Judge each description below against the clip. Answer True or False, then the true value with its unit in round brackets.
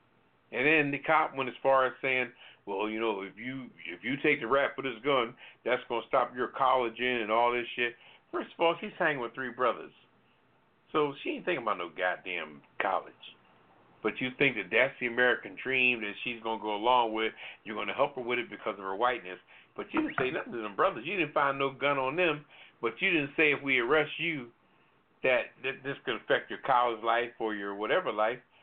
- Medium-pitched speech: False (125 Hz)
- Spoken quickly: True (230 wpm)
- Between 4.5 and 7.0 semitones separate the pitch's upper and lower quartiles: False (3.2 semitones)